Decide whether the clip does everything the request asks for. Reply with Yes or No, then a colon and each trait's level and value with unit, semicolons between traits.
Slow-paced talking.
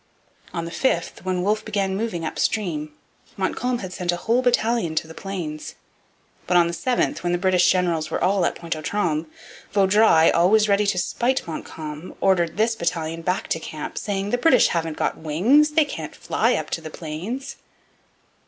No: average, 185 wpm